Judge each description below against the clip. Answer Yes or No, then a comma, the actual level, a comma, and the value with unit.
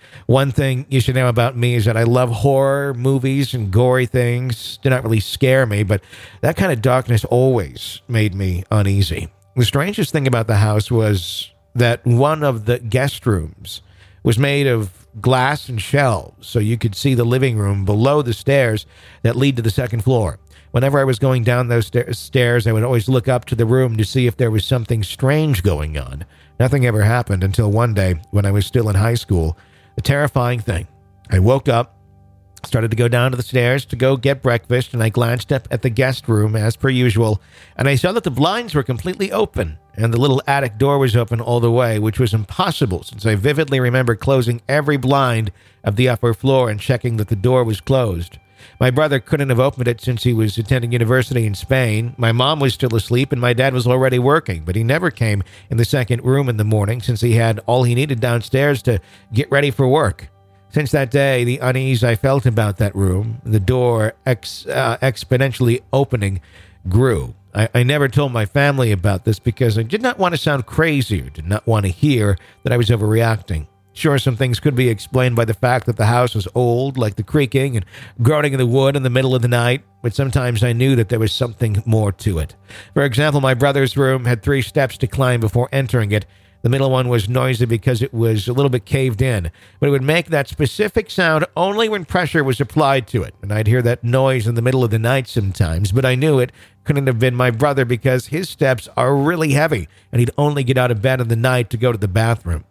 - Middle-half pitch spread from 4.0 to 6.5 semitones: No, average, 3.4 semitones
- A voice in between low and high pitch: No, low, 120 Hz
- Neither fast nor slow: No, fast, 225 wpm